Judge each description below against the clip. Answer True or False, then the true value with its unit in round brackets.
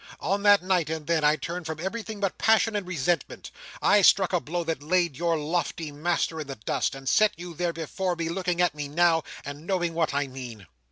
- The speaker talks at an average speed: False (220 wpm)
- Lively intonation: False (3.2 semitones)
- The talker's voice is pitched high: False (170 Hz)